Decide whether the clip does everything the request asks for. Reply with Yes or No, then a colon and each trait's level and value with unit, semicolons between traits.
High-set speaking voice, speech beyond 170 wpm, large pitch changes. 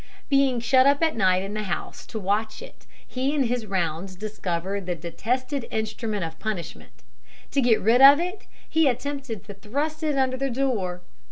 Yes: high, 225 Hz; average, 180 wpm; wide, 5.7 semitones